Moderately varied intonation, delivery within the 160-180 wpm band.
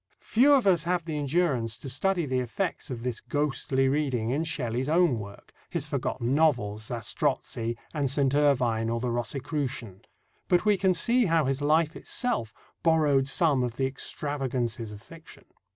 Yes: average, 5.0 semitones; average, 165 wpm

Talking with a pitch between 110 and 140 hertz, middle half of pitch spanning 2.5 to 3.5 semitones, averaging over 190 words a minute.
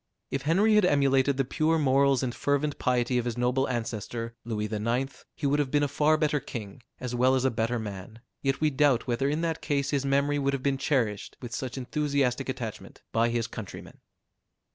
Yes: low, 135 Hz; average, 3.1 semitones; fast, 205 wpm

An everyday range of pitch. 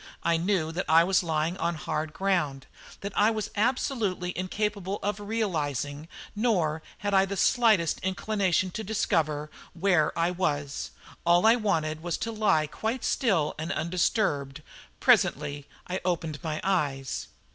Yes: average, 4.7 semitones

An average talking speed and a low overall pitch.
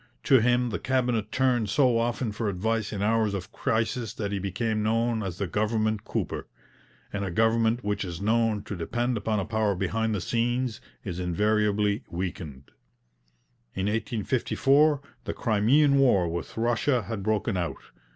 Yes: average, 160 wpm; low, 110 Hz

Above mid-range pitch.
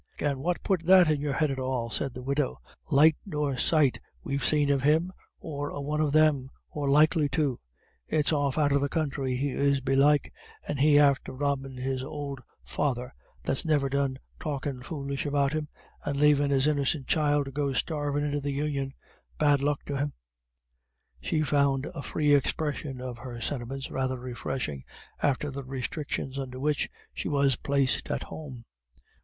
No: medium, 140 Hz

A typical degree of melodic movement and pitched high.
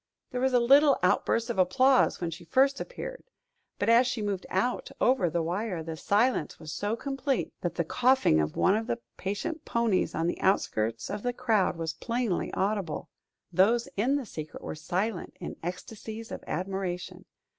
No: wide, 5.9 semitones; high, 210 Hz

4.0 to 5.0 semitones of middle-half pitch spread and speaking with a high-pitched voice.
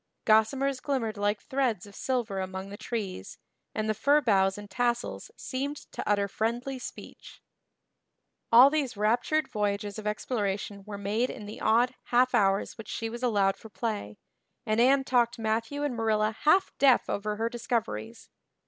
No: average, 3.4 semitones; high, 225 Hz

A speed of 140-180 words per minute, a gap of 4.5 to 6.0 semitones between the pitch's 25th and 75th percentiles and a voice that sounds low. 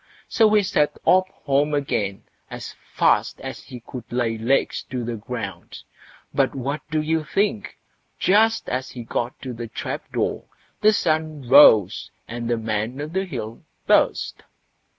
Yes: average, 155 wpm; average, 5.1 semitones; low, 130 Hz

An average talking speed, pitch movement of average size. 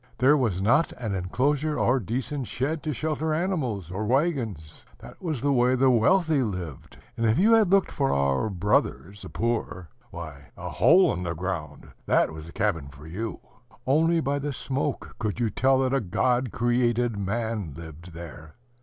No: average, 180 wpm; wide, 7.4 semitones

